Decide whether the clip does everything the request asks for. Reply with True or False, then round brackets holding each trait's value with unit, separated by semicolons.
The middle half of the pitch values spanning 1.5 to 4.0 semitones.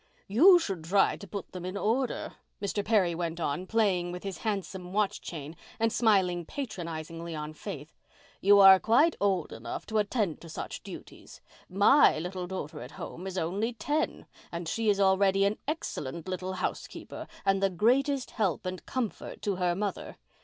True (3.5 semitones)